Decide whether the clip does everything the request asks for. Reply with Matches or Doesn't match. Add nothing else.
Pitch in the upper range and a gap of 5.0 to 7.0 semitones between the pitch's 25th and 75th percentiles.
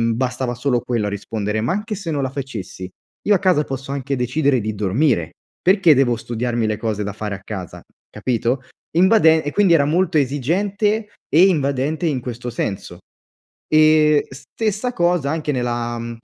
Doesn't match